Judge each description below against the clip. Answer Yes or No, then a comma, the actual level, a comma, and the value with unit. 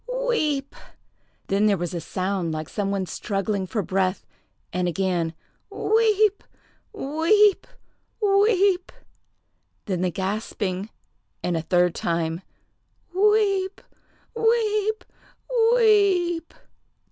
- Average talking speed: No, slow, 95 wpm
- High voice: Yes, high, 220 Hz